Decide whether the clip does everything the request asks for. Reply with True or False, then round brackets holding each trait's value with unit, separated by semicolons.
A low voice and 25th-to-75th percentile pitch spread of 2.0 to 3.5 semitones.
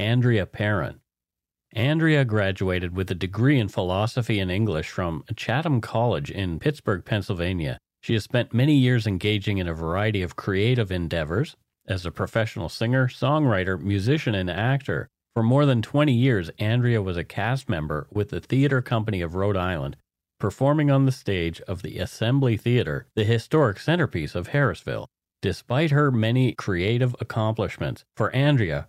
False (110 Hz; 5.2 semitones)